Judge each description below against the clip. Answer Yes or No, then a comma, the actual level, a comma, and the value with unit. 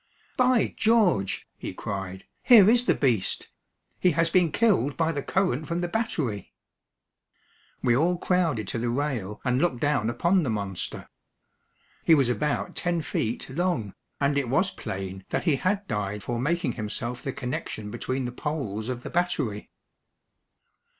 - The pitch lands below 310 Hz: Yes, low, 135 Hz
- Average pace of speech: Yes, average, 155 wpm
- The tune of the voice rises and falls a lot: Yes, wide, 7.4 semitones